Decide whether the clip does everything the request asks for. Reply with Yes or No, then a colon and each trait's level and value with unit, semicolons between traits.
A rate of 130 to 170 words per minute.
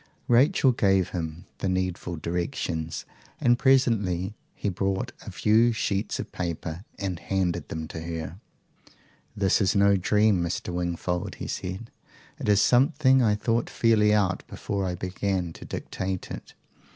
Yes: average, 145 wpm